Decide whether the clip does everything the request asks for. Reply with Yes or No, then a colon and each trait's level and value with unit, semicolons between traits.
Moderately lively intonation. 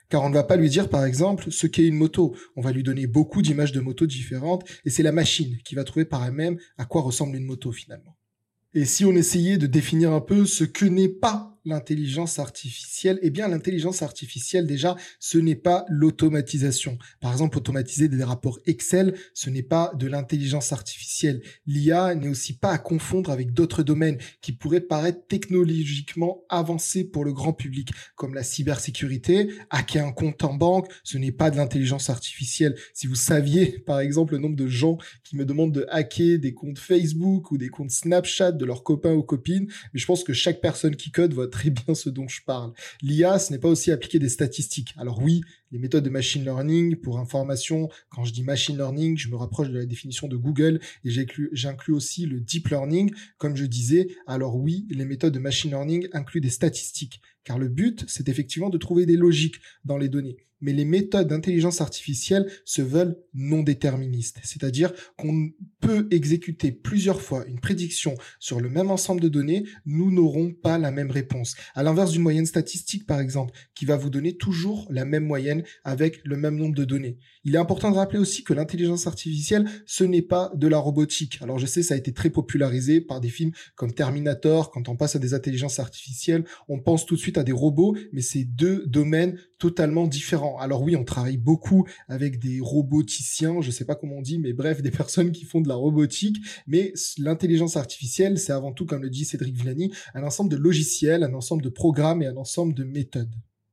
Yes: average, 3.9 semitones